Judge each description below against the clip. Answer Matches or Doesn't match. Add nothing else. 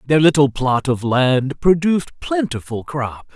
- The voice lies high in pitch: Doesn't match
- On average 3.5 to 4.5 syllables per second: Matches